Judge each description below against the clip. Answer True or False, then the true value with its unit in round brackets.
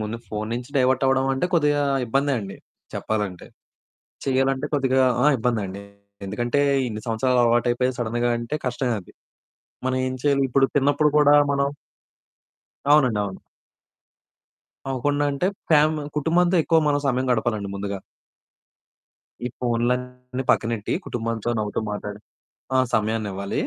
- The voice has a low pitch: True (125 Hz)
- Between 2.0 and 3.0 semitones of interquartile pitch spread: False (3.7 semitones)